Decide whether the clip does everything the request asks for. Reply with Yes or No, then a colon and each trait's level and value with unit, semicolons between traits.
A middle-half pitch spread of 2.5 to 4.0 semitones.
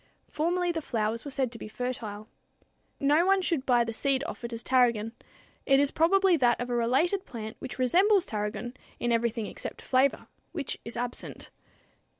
No: average, 5.1 semitones